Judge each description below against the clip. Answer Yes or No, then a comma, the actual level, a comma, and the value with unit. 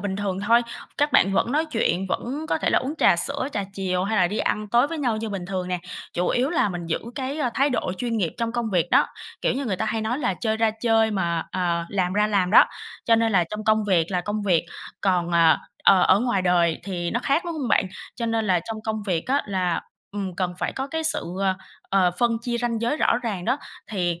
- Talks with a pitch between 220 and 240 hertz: No, high, 210 Hz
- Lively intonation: No, average, 4.7 semitones